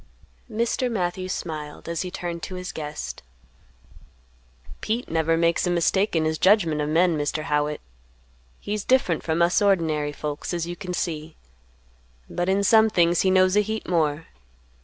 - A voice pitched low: No, medium, 175 Hz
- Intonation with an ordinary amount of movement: Yes, average, 3.3 semitones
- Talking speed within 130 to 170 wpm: Yes, average, 160 wpm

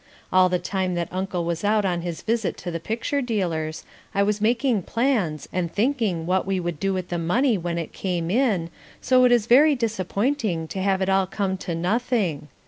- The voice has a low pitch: No, high, 190 Hz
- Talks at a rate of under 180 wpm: No, fast, 205 wpm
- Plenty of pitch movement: No, average, 4.6 semitones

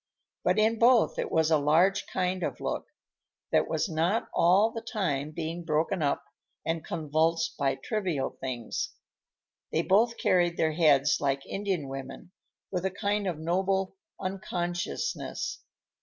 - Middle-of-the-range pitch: Yes, medium, 175 Hz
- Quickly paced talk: No, average, 140 wpm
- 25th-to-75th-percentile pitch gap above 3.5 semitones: Yes, average, 4.0 semitones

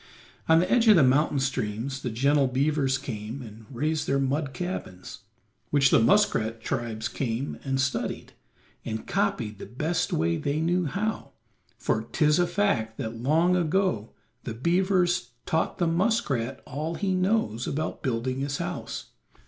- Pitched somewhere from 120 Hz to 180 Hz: Yes, medium, 140 Hz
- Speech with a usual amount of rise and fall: No, wide, 6.4 semitones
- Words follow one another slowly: No, average, 155 wpm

